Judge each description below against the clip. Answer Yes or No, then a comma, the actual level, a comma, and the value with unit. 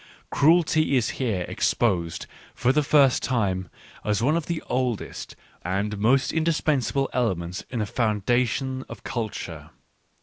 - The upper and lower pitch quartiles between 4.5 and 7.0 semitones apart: Yes, average, 4.8 semitones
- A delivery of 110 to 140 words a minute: Yes, slow, 135 wpm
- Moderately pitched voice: No, low, 120 Hz